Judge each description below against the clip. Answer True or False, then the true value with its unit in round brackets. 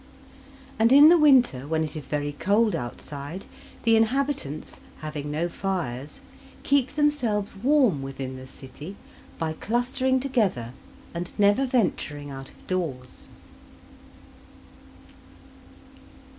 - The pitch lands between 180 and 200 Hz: True (185 Hz)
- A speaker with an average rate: False (110 wpm)